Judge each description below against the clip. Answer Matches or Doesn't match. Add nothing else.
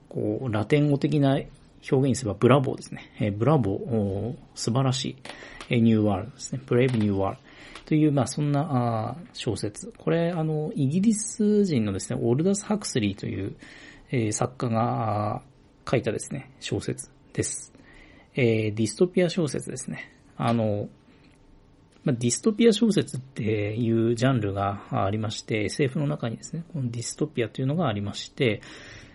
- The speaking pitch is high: Doesn't match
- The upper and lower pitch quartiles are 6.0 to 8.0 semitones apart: Doesn't match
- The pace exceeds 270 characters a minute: Matches